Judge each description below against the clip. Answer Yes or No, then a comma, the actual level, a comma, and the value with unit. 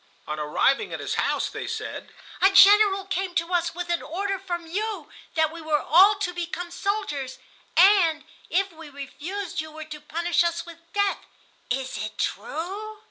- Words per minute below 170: No, average, 175 wpm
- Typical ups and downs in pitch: Yes, average, 3.8 semitones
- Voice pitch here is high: Yes, very high, 345 Hz